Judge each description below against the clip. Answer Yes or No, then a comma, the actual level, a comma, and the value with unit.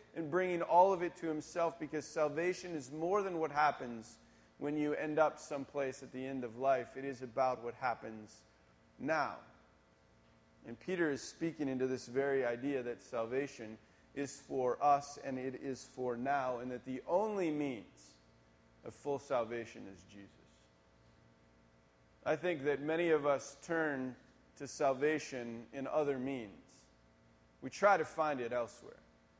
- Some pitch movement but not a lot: No, wide, 7.3 semitones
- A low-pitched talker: Yes, low, 130 Hz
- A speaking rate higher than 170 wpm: No, average, 155 wpm